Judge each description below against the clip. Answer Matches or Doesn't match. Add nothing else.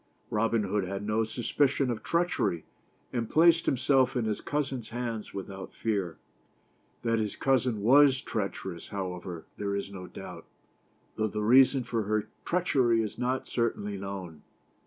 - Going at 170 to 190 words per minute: Doesn't match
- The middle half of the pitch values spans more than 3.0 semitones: Matches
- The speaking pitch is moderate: Doesn't match